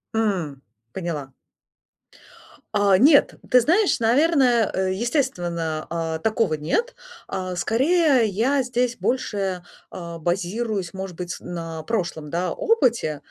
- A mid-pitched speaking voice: No, high, 195 Hz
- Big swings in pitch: Yes, wide, 6.4 semitones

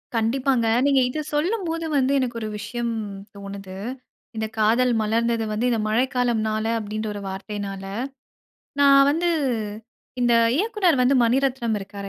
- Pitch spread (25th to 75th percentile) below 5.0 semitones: Yes, average, 4.1 semitones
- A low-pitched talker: No, high, 235 Hz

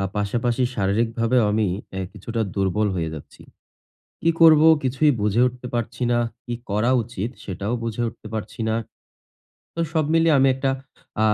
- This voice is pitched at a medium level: No, low, 115 Hz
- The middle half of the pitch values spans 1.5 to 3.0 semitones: No, average, 3.4 semitones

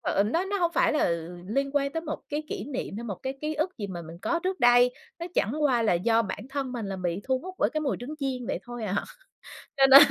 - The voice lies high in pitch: Yes, very high, 260 Hz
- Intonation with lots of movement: Yes, wide, 5.7 semitones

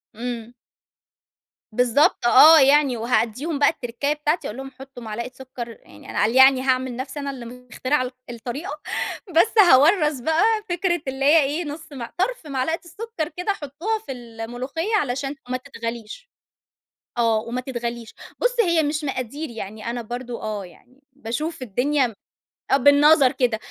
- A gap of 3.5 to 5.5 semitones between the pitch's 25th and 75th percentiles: Yes, average, 4.0 semitones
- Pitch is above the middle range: Yes, very high, 265 Hz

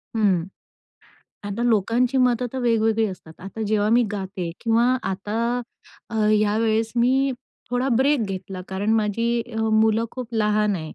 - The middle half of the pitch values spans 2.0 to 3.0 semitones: Yes, narrow, 2.5 semitones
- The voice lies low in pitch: No, high, 220 Hz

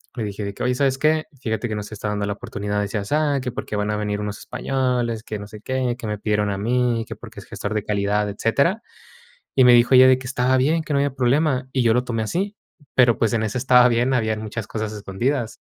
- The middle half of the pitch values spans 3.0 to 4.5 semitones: Yes, average, 3.7 semitones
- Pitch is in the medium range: No, low, 120 Hz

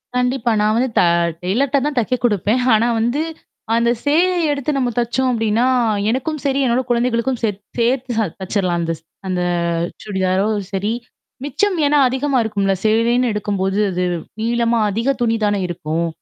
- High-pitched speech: Yes, high, 235 Hz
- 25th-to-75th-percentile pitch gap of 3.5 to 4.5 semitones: Yes, average, 3.9 semitones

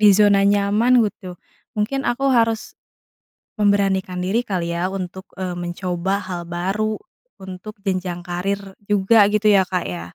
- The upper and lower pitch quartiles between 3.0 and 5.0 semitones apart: No, narrow, 2.5 semitones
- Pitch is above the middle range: Yes, high, 195 Hz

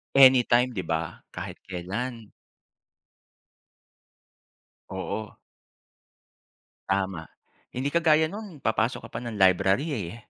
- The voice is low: Yes, low, 115 Hz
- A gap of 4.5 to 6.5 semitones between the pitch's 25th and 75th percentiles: Yes, wide, 5.6 semitones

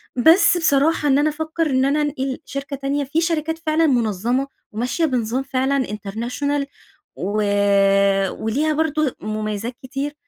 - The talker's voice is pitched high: Yes, very high, 275 Hz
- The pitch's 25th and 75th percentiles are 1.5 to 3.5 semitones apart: No, average, 3.9 semitones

